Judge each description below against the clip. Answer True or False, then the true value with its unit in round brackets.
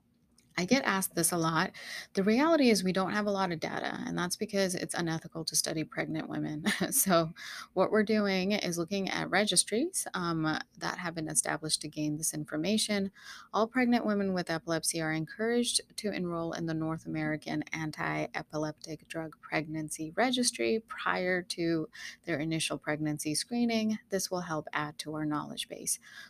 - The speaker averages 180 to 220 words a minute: False (170 wpm)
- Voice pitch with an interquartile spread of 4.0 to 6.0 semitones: True (4.3 semitones)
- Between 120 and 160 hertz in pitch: False (170 Hz)